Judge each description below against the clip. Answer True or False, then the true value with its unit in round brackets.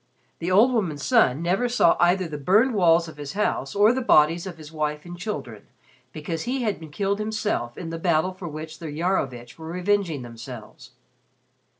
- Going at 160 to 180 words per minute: False (190 wpm)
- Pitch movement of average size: True (4.9 semitones)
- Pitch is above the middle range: False (170 Hz)